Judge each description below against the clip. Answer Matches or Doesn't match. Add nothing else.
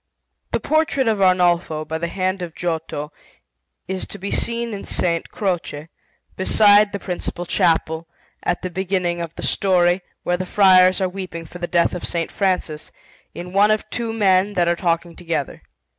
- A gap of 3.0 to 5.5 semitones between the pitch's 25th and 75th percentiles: Doesn't match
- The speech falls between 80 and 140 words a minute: Doesn't match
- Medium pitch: Matches